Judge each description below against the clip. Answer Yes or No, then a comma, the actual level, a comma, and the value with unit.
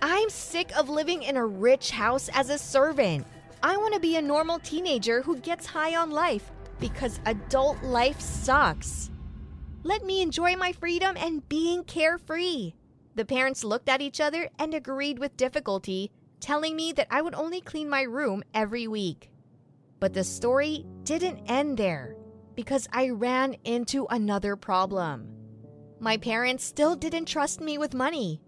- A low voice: No, very high, 270 Hz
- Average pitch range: No, wide, 7.0 semitones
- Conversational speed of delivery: Yes, average, 160 wpm